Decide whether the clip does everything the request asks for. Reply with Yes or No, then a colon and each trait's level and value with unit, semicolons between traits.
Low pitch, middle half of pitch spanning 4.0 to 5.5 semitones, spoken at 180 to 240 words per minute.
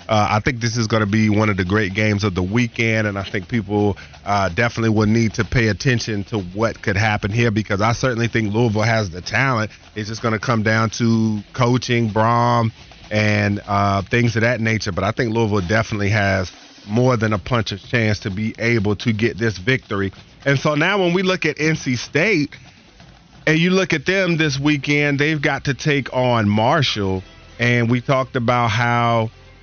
No: low, 115 Hz; average, 3.0 semitones; fast, 205 wpm